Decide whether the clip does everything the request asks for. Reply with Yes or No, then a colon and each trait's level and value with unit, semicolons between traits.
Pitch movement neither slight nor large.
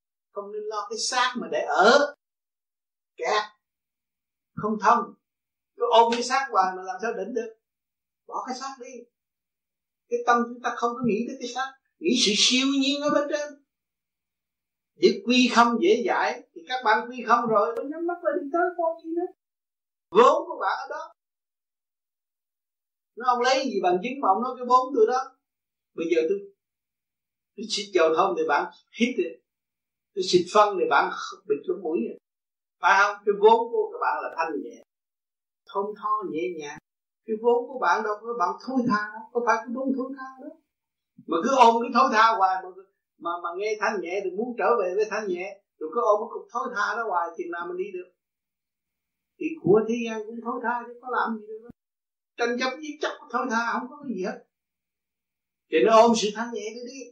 Yes: average, 4.3 semitones